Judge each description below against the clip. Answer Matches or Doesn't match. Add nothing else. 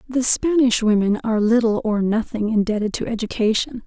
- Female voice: Matches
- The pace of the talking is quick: Doesn't match